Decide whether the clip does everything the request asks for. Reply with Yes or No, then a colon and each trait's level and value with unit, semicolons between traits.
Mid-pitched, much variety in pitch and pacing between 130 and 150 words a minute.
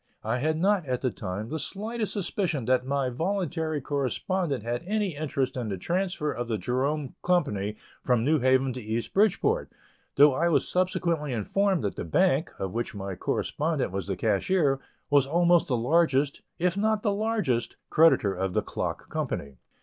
No: medium, 145 Hz; wide, 6.8 semitones; average, 175 wpm